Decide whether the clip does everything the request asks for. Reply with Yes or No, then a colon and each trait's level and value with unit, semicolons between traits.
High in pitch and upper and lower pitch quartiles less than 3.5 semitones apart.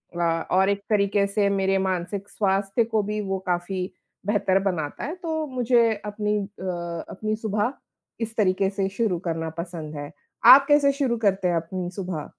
Yes: high, 195 Hz; average, 3.1 semitones